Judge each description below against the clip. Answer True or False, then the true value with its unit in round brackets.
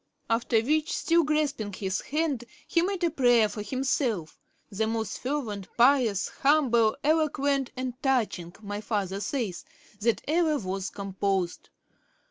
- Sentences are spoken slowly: True (130 wpm)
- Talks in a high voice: True (240 Hz)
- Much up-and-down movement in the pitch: True (5.9 semitones)